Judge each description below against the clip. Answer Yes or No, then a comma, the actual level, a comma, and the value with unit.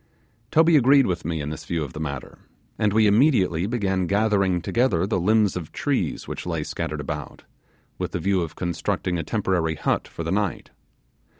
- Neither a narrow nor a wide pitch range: Yes, average, 4.5 semitones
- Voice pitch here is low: Yes, very low, 95 Hz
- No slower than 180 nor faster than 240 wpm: Yes, average, 185 wpm